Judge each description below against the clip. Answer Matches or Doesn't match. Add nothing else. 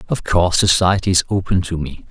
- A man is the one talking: Matches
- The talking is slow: Doesn't match